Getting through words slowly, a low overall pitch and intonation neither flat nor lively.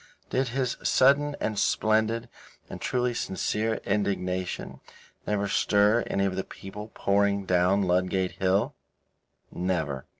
Yes: slow, 120 wpm; low, 100 Hz; average, 3.1 semitones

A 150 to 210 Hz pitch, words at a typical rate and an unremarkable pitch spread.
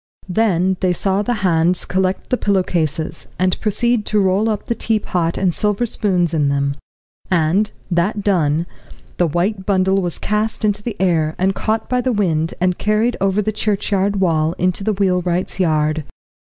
Yes: high, 190 Hz; average, 170 wpm; average, 3.4 semitones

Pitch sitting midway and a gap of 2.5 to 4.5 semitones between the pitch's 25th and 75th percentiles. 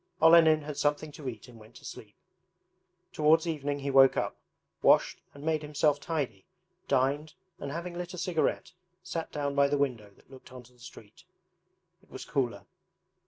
Yes: medium, 145 Hz; average, 3.2 semitones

